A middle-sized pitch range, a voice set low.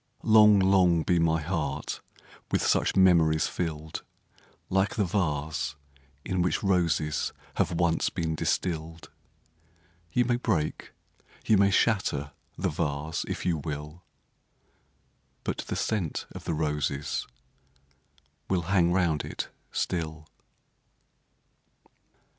Yes: average, 3.2 semitones; very low, 85 Hz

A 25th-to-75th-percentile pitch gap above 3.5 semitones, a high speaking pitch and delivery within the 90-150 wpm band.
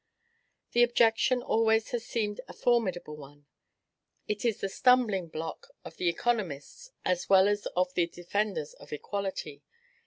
Yes: average, 4.8 semitones; high, 200 Hz; average, 145 wpm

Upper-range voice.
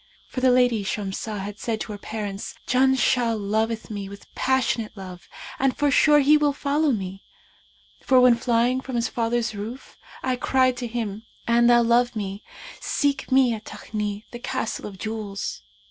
Yes: high, 235 Hz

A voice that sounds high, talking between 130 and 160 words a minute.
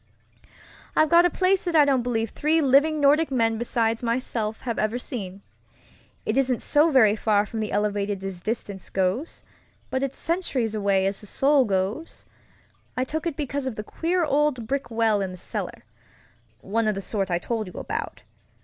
No: high, 235 Hz; average, 180 wpm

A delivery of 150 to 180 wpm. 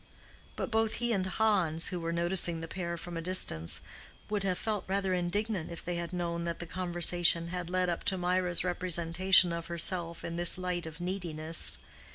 No: average, 190 wpm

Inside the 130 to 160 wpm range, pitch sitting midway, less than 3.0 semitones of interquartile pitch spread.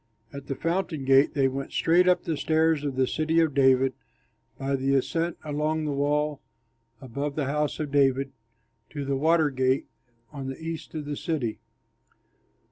No: average, 170 wpm; medium, 145 Hz; narrow, 2.6 semitones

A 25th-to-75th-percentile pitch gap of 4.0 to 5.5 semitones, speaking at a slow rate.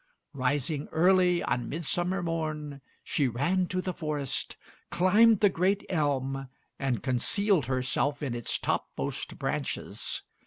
Yes: average, 5.2 semitones; slow, 120 wpm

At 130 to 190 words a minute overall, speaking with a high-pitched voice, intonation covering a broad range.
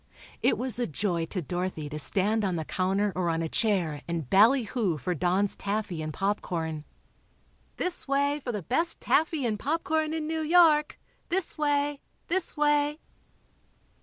Yes: average, 160 wpm; high, 210 Hz; wide, 8.9 semitones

